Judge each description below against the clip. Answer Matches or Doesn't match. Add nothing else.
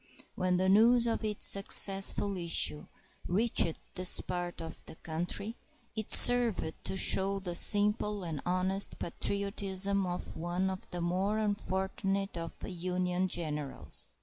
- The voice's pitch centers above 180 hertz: Matches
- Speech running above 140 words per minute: Doesn't match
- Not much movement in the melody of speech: Matches